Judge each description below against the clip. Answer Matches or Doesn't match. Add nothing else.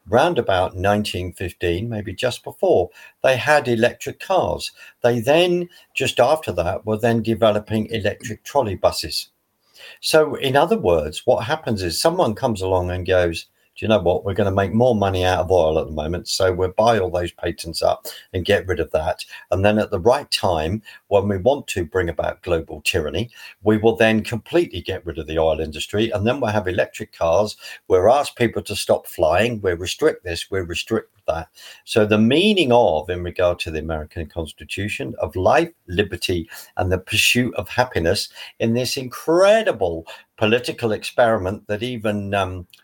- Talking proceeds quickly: Doesn't match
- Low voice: Matches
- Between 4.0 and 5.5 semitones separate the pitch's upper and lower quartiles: Matches